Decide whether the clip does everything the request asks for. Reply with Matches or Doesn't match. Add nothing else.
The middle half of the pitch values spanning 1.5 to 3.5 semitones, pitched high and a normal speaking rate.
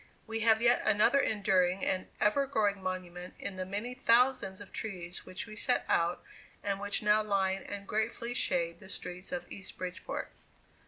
Matches